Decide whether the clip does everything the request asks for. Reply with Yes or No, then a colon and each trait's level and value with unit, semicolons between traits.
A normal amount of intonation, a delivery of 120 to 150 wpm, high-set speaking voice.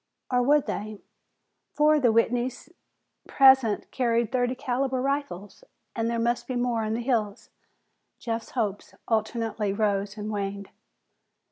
Yes: average, 3.0 semitones; slow, 135 wpm; high, 235 Hz